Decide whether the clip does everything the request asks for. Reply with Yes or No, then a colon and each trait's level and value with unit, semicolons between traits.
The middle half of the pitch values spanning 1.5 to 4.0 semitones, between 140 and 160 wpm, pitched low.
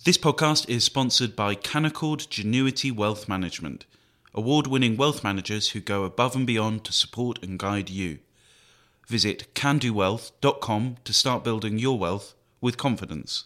No: average, 4.4 semitones; average, 145 wpm; low, 115 Hz